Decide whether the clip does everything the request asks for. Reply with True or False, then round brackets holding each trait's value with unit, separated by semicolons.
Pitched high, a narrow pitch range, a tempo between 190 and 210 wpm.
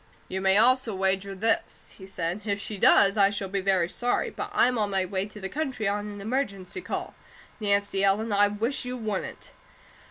True (200 Hz; 2.3 semitones; 195 wpm)